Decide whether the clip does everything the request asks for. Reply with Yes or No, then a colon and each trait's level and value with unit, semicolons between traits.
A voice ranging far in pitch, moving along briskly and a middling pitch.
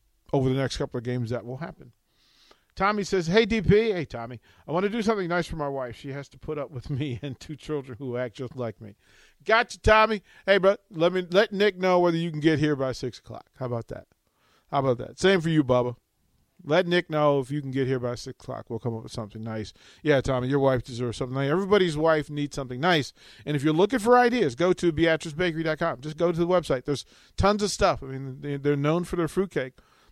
Yes: wide, 6.0 semitones; fast, 240 wpm; medium, 145 Hz